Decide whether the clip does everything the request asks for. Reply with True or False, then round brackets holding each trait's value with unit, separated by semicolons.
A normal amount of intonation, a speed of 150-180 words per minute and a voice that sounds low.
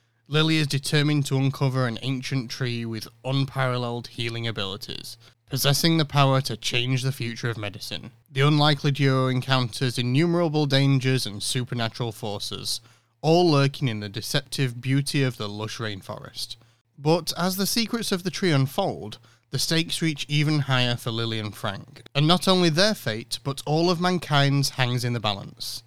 True (4.1 semitones; 160 wpm; 130 Hz)